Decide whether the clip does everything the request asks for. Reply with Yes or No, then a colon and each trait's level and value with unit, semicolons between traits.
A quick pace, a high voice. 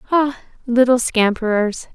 No: slow, 95 wpm; high, 240 Hz